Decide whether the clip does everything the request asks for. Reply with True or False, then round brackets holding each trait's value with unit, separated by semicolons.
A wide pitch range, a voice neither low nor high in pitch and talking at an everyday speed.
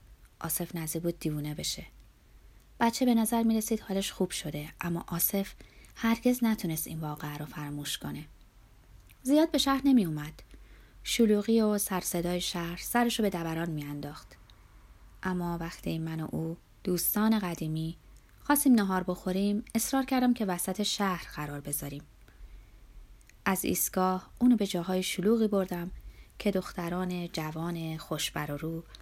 False (5.0 semitones; 175 Hz; 135 wpm)